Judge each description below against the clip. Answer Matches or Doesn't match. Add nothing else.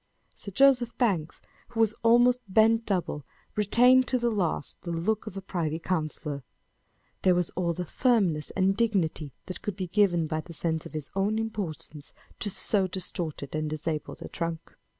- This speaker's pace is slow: Doesn't match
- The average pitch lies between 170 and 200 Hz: Matches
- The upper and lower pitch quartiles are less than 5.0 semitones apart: Doesn't match